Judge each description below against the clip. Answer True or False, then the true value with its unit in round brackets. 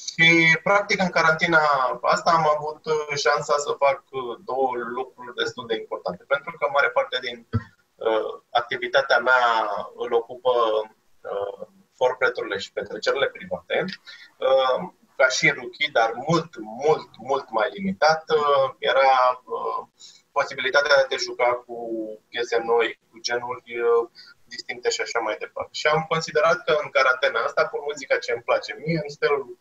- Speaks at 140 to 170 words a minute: True (145 wpm)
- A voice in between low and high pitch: True (155 Hz)